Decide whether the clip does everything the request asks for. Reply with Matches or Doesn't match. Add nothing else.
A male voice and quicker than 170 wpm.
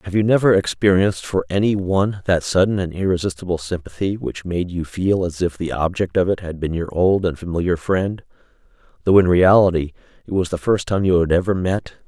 Matches